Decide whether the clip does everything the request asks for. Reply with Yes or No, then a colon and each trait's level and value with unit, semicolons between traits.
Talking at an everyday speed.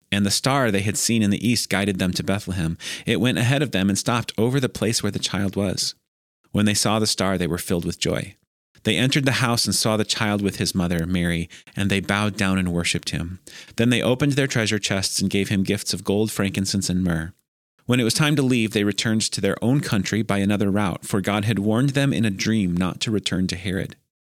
No: fast, 245 wpm